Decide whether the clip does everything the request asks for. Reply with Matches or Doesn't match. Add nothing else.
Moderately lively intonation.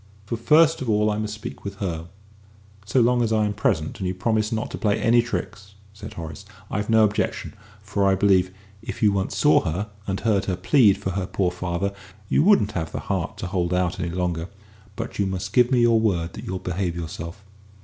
Matches